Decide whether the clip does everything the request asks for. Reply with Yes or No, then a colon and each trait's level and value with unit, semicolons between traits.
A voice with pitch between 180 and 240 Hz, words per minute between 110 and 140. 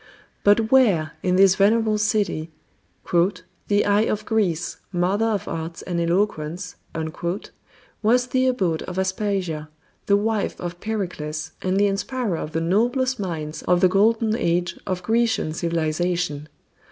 Yes: high, 190 Hz; slow, 135 wpm